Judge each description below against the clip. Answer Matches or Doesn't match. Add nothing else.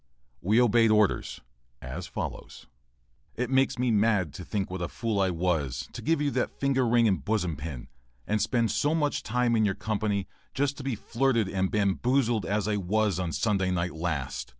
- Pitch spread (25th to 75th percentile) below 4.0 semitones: Doesn't match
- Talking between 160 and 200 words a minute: Matches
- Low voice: Matches